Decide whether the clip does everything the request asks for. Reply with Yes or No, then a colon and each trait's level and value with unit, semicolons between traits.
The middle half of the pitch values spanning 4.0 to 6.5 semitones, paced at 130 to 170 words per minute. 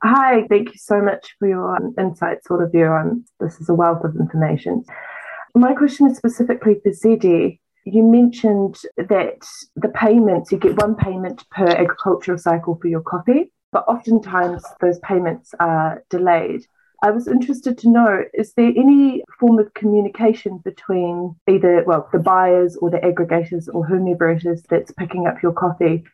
Yes: average, 4.7 semitones; average, 160 wpm